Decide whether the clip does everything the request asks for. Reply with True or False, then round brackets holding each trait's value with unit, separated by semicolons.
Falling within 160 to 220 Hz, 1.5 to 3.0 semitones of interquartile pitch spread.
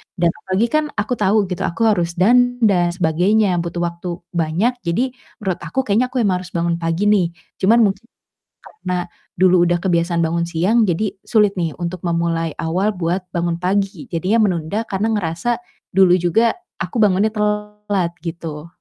False (185 Hz; 3.6 semitones)